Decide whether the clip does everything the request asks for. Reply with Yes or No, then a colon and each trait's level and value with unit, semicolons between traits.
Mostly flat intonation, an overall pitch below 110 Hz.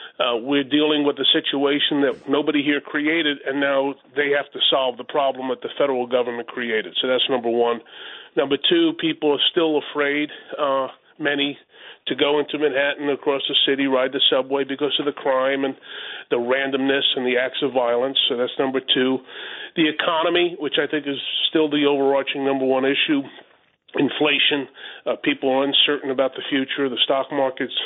No: narrow, 1.9 semitones; medium, 140 Hz